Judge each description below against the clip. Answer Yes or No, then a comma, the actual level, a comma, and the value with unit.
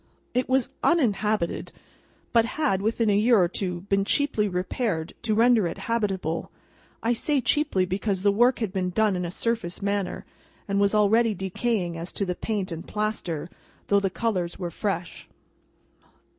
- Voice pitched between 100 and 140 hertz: No, high, 200 Hz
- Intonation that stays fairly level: No, average, 3.9 semitones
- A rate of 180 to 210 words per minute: No, average, 165 wpm